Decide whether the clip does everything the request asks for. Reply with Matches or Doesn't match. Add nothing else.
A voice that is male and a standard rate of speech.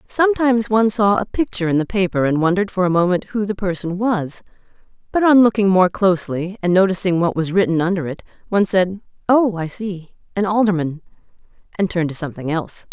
Doesn't match